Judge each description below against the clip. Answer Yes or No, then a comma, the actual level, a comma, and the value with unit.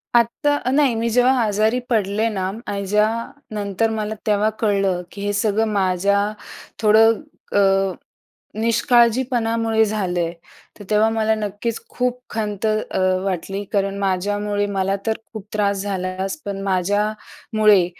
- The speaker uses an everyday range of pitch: No, narrow, 2.1 semitones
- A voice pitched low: No, high, 210 Hz